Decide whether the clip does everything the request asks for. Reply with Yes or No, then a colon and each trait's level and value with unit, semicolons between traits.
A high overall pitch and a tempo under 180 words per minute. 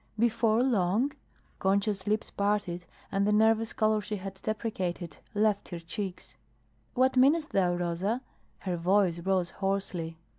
Yes: high, 200 Hz; slow, 135 wpm